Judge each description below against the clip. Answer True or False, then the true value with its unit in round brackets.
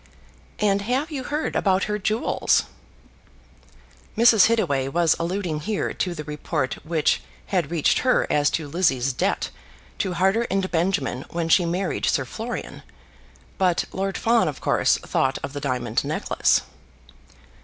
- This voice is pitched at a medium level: True (175 Hz)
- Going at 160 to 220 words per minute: False (145 wpm)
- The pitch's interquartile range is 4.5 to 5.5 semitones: True (5.2 semitones)